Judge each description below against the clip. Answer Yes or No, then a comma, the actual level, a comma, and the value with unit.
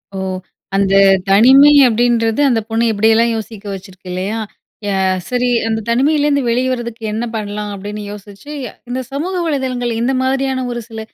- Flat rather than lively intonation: No, average, 3.7 semitones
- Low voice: No, high, 230 Hz